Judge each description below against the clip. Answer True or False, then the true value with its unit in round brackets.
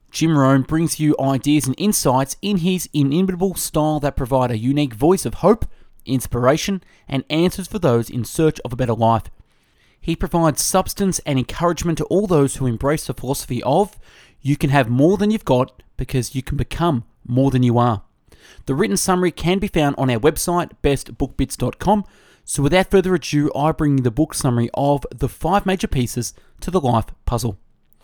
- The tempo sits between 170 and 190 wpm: True (185 wpm)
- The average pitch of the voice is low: False (145 Hz)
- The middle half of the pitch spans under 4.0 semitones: False (5.1 semitones)